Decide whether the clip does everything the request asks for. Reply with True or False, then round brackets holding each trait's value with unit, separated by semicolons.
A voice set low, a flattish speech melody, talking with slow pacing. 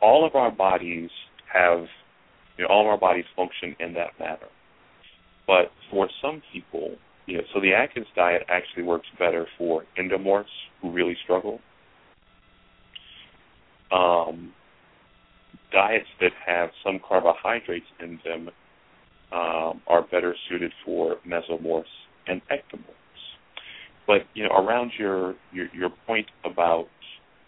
True (85 Hz; 1.7 semitones; 125 wpm)